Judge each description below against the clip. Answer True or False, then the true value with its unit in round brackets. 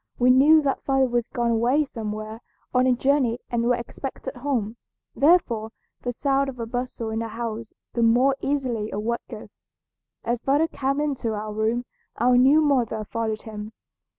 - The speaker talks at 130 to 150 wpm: False (170 wpm)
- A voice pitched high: True (240 Hz)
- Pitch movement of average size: True (3.1 semitones)